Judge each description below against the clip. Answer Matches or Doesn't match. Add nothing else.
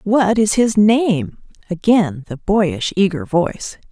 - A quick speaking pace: Doesn't match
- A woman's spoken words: Matches